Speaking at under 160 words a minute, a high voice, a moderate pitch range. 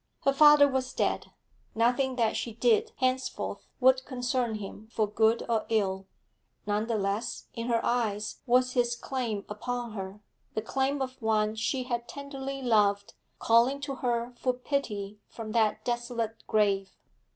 Yes: average, 150 wpm; high, 235 Hz; average, 3.2 semitones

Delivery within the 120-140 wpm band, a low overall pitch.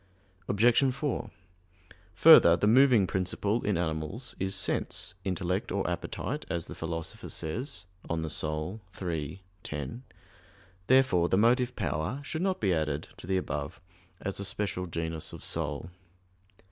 Yes: slow, 135 wpm; very low, 95 Hz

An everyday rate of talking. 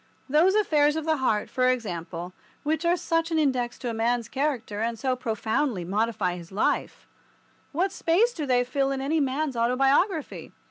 Yes: average, 170 wpm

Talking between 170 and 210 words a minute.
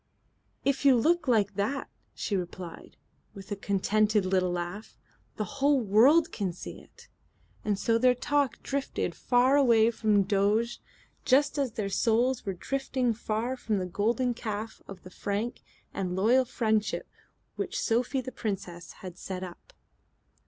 No: average, 150 wpm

